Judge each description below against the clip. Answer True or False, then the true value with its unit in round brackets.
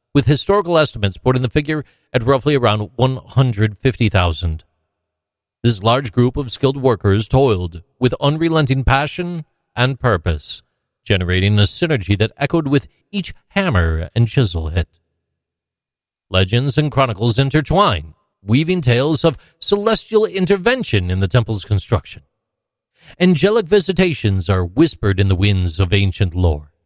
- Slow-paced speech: True (125 wpm)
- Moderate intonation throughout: False (7.3 semitones)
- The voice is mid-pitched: False (120 Hz)